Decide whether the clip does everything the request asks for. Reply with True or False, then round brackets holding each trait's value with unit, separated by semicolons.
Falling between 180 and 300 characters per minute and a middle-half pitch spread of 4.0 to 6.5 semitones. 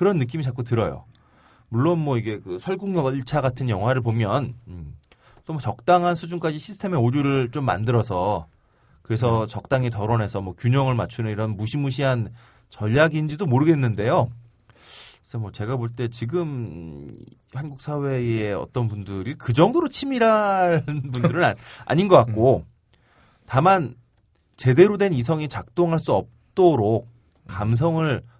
True (295 characters per minute; 5.4 semitones)